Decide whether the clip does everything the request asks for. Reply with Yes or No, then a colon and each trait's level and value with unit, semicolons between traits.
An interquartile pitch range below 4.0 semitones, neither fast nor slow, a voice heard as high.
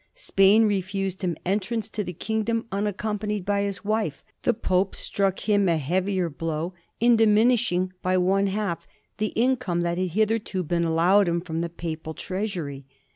Yes: average, 3.5 semitones; average, 170 wpm; high, 195 Hz